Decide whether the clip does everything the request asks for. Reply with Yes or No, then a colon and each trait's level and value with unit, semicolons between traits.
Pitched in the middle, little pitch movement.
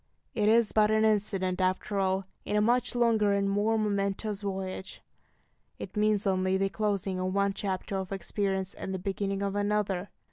No: high, 200 Hz; narrow, 1.7 semitones